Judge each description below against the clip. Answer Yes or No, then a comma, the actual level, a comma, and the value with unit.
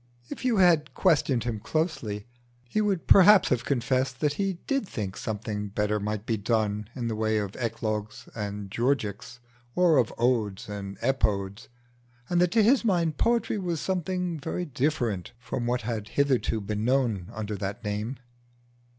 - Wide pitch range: Yes, wide, 7.2 semitones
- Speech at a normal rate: Yes, average, 160 wpm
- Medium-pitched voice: No, low, 120 Hz